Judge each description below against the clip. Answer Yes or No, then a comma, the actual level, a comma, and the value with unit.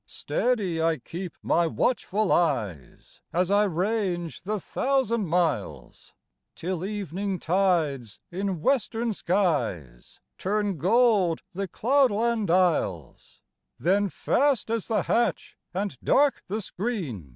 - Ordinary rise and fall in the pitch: Yes, average, 4.5 semitones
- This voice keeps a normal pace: No, slow, 110 wpm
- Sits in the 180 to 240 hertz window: Yes, high, 190 Hz